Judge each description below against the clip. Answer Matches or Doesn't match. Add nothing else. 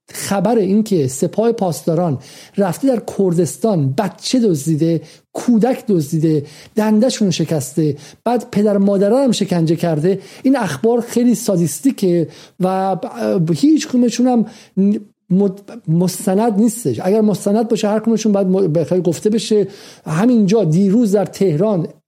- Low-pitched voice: Doesn't match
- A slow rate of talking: Doesn't match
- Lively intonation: Doesn't match